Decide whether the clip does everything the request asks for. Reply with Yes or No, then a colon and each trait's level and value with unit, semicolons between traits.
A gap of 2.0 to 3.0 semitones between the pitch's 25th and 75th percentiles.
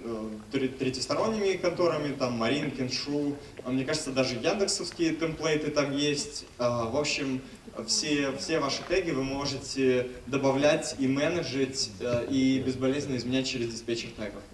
Yes: average, 2.7 semitones